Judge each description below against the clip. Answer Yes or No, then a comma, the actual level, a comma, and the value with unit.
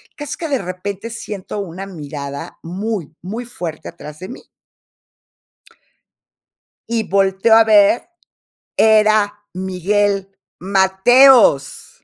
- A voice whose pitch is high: Yes, high, 195 Hz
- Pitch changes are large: No, average, 3.2 semitones